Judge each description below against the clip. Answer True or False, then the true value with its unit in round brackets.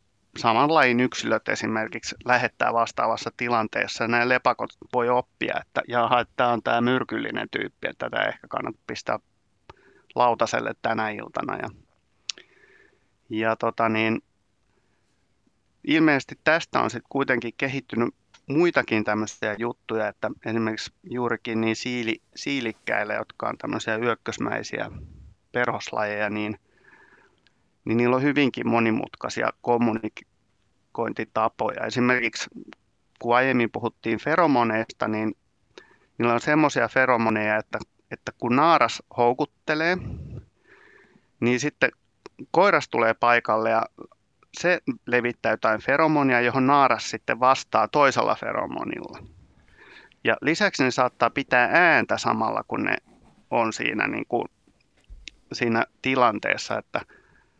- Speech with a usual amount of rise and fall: False (2.2 semitones)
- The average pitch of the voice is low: True (120 Hz)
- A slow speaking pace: False (105 wpm)